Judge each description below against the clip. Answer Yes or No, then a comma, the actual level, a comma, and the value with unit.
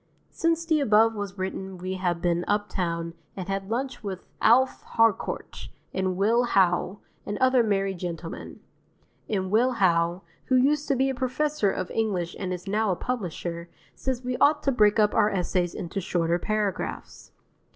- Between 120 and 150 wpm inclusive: No, average, 165 wpm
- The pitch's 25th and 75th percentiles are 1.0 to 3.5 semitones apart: No, average, 5.0 semitones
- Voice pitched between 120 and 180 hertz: No, high, 200 Hz